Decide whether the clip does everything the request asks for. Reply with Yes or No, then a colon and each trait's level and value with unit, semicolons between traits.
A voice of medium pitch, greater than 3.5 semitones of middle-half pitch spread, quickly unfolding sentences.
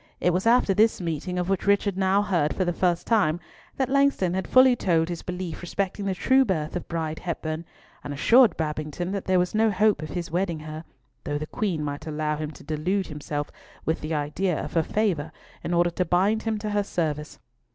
Yes: medium, 175 Hz; average, 4.2 semitones; fast, 215 wpm